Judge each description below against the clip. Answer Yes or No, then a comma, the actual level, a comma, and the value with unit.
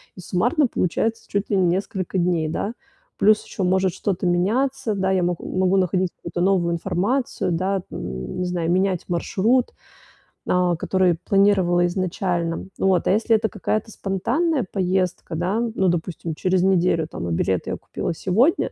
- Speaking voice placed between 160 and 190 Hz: Yes, medium, 185 Hz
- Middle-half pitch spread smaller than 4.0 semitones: Yes, narrow, 2.5 semitones